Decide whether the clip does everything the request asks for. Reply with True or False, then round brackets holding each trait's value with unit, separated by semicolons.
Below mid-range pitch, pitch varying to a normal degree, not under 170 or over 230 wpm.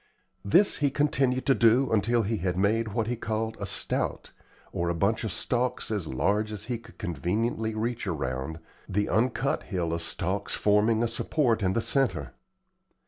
True (110 Hz; 3.9 semitones; 175 wpm)